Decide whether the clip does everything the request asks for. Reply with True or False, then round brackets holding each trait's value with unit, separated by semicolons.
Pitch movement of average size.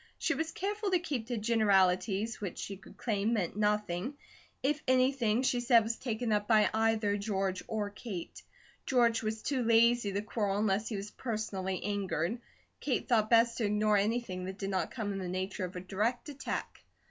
True (3.1 semitones)